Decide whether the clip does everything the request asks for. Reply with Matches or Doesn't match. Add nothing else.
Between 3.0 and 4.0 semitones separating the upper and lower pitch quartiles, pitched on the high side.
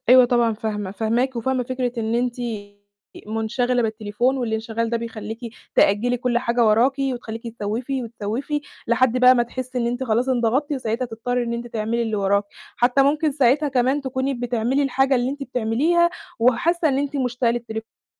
Doesn't match